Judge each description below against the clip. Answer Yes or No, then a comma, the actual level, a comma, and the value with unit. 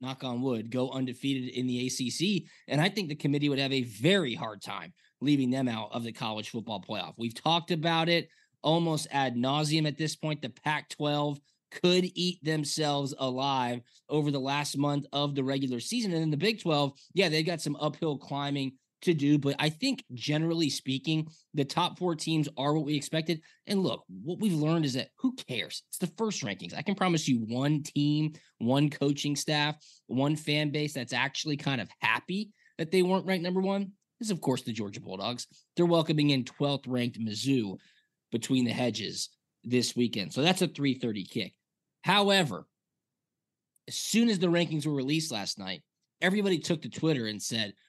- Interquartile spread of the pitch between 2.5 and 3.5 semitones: No, average, 4.3 semitones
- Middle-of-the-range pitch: Yes, medium, 150 Hz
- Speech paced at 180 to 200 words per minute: Yes, average, 190 wpm